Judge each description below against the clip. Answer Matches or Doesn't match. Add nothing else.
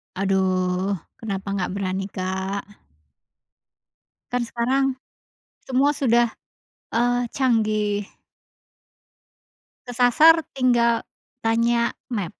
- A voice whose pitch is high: Matches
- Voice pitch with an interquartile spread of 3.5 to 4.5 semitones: Matches